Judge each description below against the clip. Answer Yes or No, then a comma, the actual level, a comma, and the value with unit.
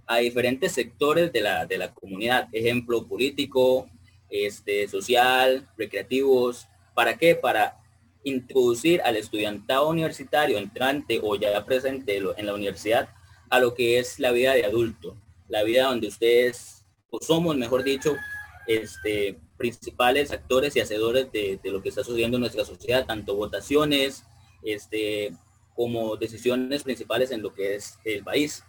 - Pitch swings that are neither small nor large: Yes, average, 4.5 semitones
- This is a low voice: Yes, low, 120 Hz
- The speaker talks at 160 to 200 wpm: No, average, 145 wpm